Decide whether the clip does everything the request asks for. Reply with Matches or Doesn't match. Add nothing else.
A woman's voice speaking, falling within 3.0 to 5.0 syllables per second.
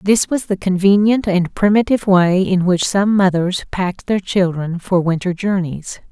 Matches